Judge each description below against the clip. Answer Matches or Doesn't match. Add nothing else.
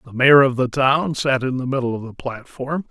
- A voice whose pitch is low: Matches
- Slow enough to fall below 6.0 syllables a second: Matches